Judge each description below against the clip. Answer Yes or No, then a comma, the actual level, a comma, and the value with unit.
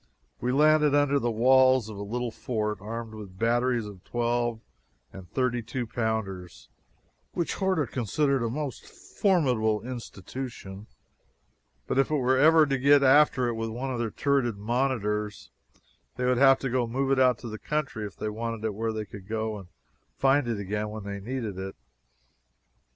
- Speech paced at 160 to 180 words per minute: Yes, average, 175 wpm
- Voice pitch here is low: Yes, low, 120 Hz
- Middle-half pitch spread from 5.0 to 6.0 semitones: No, average, 3.8 semitones